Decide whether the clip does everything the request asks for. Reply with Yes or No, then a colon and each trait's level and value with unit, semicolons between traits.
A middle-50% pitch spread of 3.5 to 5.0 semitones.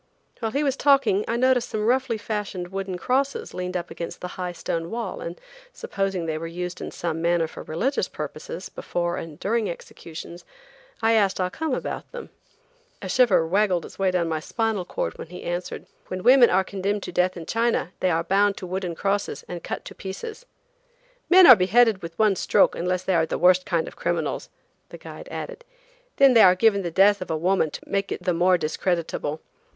Yes: average, 4.3 semitones